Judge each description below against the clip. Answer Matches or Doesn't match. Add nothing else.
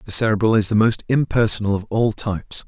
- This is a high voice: Doesn't match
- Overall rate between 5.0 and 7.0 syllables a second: Matches